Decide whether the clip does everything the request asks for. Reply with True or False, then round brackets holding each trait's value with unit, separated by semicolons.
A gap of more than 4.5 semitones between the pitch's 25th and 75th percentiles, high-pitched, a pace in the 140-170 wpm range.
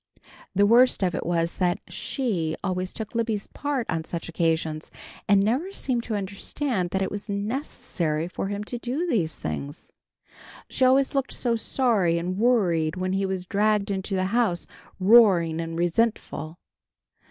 True (5.2 semitones; 195 Hz; 160 wpm)